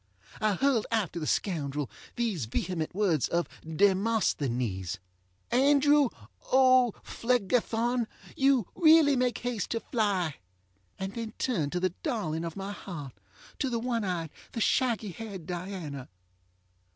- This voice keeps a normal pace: No, slow, 125 wpm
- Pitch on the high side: Yes, high, 205 Hz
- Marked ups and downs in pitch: Yes, wide, 6.5 semitones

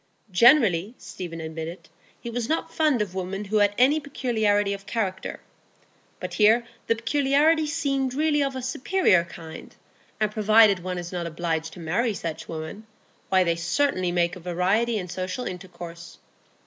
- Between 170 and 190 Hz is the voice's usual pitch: No, high, 205 Hz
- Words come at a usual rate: Yes, average, 160 wpm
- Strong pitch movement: Yes, wide, 6.0 semitones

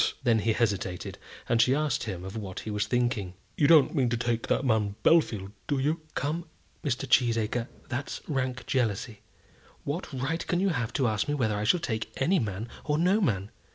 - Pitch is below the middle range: Yes, low, 120 Hz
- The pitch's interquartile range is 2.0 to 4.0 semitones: No, average, 4.9 semitones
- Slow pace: No, average, 195 wpm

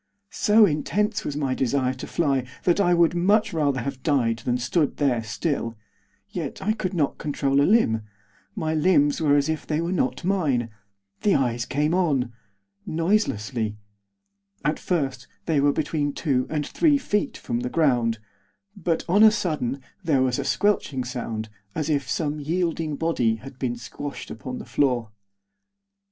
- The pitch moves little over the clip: No, average, 4.9 semitones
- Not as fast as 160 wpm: No, average, 165 wpm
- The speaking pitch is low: No, medium, 145 Hz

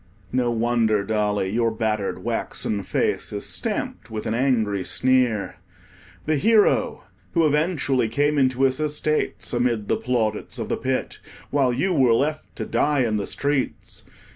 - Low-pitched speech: Yes, low, 125 Hz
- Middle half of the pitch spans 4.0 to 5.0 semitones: Yes, average, 4.5 semitones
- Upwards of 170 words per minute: No, average, 150 wpm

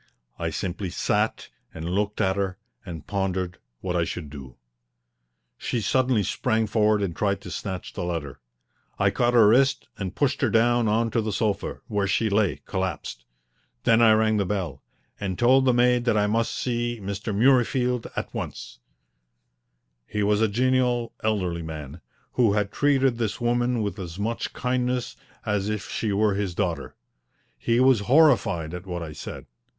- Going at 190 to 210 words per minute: No, average, 170 wpm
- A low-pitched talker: Yes, low, 105 Hz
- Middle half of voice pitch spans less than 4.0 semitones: No, average, 4.3 semitones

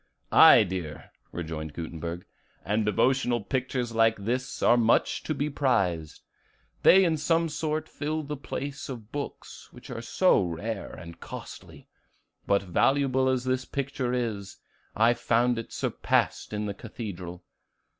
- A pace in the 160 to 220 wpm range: No, average, 140 wpm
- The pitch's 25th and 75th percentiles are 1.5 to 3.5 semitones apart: No, average, 5.3 semitones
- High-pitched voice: No, low, 120 Hz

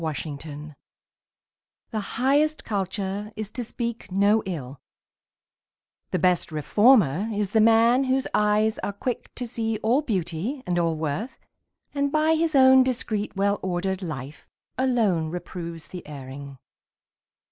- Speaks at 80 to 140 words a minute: Yes, slow, 135 wpm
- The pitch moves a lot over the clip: Yes, wide, 6.4 semitones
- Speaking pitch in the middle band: No, high, 205 Hz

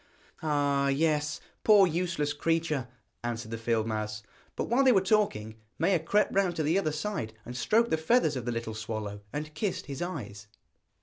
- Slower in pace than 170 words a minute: No, average, 180 wpm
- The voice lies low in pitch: No, medium, 150 Hz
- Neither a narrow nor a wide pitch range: No, wide, 7.6 semitones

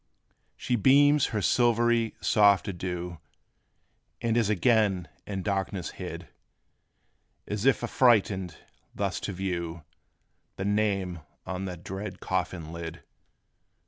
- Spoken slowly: Yes, slow, 110 wpm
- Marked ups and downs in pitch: No, average, 4.0 semitones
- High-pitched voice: No, low, 100 Hz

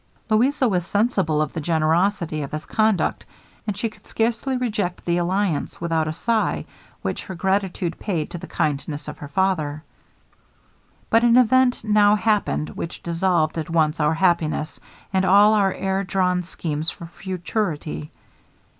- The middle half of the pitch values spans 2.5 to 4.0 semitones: No, average, 4.6 semitones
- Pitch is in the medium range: Yes, medium, 180 Hz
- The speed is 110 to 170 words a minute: Yes, average, 155 wpm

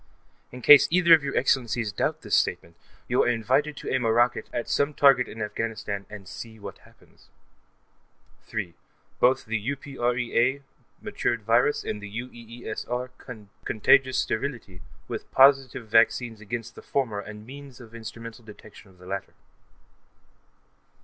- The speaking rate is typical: Yes, average, 145 wpm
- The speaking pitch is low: Yes, low, 120 Hz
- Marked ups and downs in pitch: No, average, 3.2 semitones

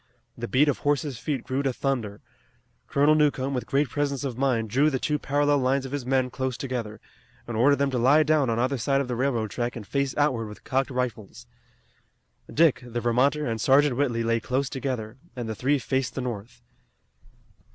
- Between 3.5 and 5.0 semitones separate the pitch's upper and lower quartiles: No, average, 2.8 semitones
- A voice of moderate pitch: No, low, 130 Hz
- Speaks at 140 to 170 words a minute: No, average, 200 wpm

